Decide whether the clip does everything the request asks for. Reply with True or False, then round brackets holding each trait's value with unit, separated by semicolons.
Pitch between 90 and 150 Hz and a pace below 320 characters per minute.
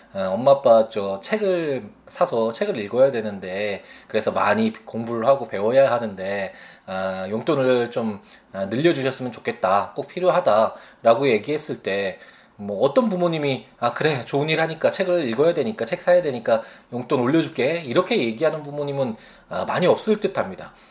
False (140 Hz; 335 characters per minute)